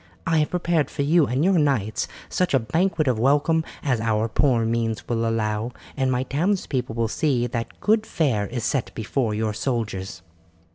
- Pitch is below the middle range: Yes, low, 125 Hz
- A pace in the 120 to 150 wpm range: No, average, 180 wpm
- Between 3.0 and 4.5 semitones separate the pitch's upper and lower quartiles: No, average, 5.1 semitones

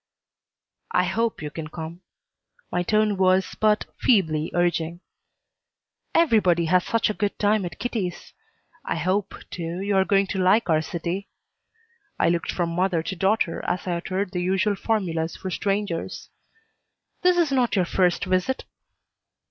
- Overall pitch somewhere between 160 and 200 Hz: Yes, medium, 185 Hz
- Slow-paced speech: No, average, 150 wpm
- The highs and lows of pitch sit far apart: No, average, 3.2 semitones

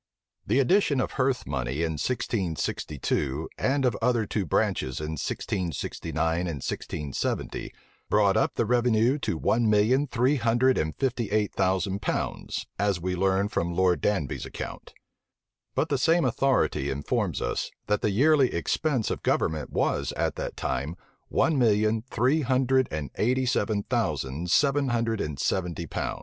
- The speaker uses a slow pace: No, average, 150 wpm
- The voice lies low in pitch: Yes, low, 105 Hz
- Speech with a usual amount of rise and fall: No, wide, 7.2 semitones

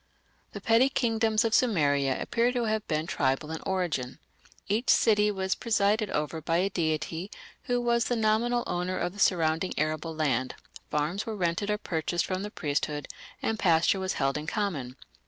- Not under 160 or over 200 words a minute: Yes, average, 175 wpm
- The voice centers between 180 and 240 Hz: Yes, medium, 185 Hz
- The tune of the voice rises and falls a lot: Yes, wide, 5.7 semitones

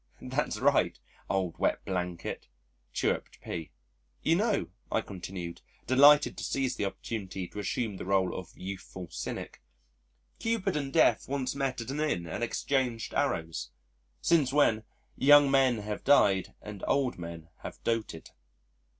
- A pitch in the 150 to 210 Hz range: No, low, 110 Hz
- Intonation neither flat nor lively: No, wide, 6.8 semitones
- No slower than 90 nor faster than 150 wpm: Yes, average, 140 wpm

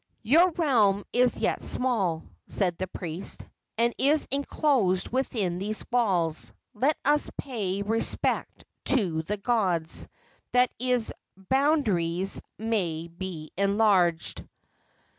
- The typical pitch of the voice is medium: No, high, 210 Hz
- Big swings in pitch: Yes, wide, 5.7 semitones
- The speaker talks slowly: Yes, slow, 105 wpm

